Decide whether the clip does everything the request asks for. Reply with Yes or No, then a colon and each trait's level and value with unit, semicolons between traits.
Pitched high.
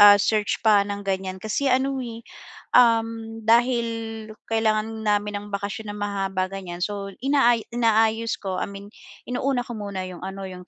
Yes: high, 215 Hz